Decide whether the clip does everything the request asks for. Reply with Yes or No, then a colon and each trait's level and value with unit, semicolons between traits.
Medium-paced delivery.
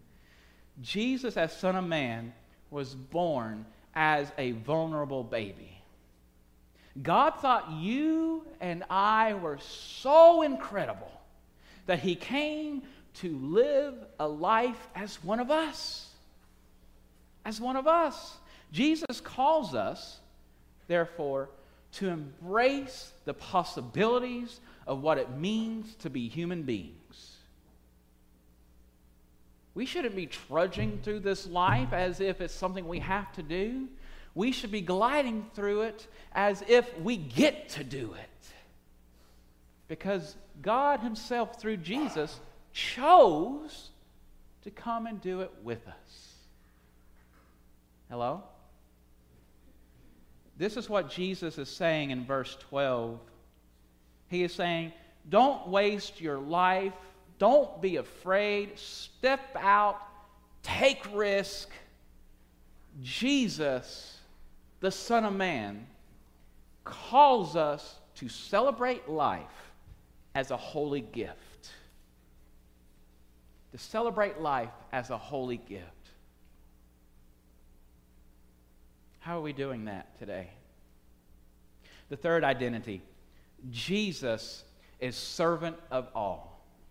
No: slow, 105 wpm